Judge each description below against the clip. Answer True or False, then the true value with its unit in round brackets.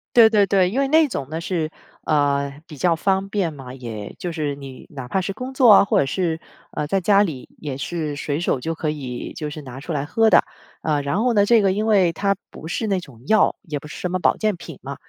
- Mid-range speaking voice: True (165 Hz)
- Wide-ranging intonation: True (5.7 semitones)